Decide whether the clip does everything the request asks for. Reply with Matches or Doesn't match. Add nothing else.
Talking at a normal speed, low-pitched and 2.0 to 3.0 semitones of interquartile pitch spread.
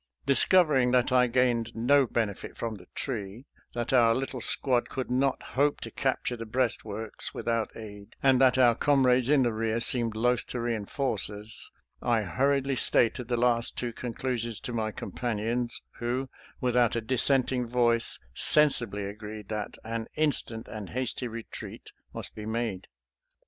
Matches